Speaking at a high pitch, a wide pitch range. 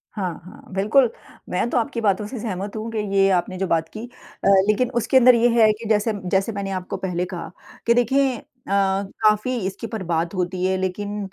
No: high, 205 Hz; average, 3.5 semitones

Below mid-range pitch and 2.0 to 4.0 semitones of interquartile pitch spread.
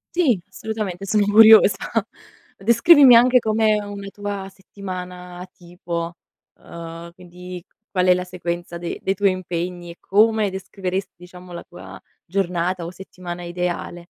No: medium, 185 Hz; average, 2.7 semitones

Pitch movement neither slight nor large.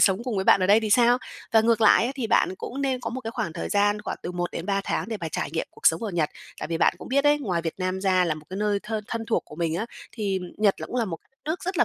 Yes: average, 4.3 semitones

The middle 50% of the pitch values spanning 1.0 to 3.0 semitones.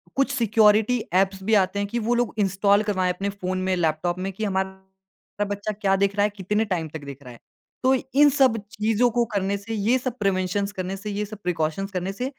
Yes: narrow, 2.4 semitones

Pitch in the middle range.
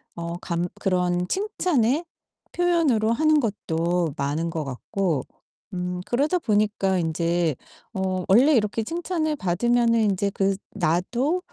No: high, 195 Hz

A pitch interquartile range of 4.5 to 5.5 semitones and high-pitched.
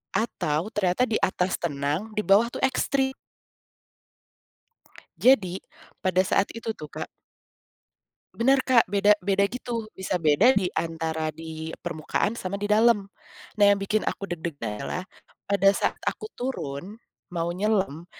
Yes: average, 4.8 semitones; high, 195 Hz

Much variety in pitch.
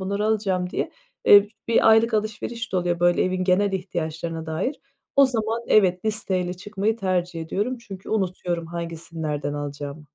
No: average, 4.0 semitones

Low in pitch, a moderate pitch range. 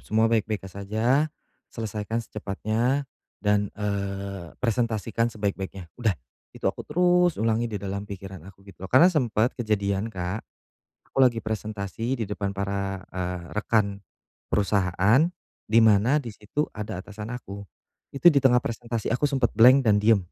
Yes: low, 110 Hz; average, 3.1 semitones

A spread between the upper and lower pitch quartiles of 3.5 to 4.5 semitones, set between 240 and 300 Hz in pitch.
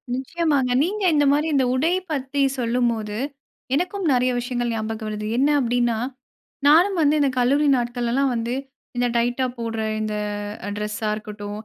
Yes: average, 3.9 semitones; high, 245 Hz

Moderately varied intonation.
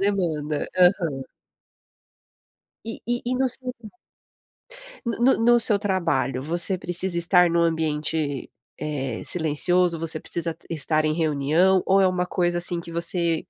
Yes: average, 3.2 semitones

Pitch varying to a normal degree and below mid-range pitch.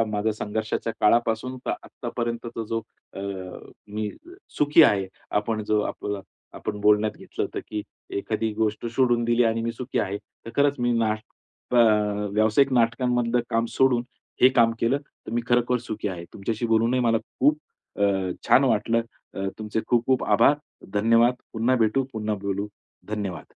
No: narrow, 2.3 semitones; low, 115 Hz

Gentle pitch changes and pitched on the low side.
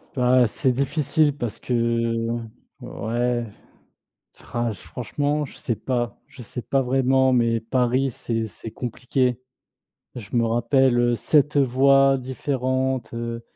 Yes: narrow, 2.2 semitones; low, 125 Hz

